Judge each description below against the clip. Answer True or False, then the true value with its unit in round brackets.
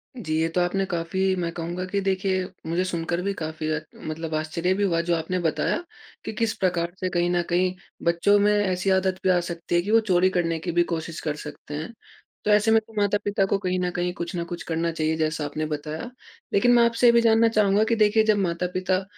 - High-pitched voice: False (180 Hz)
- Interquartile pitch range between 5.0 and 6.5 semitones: False (3.1 semitones)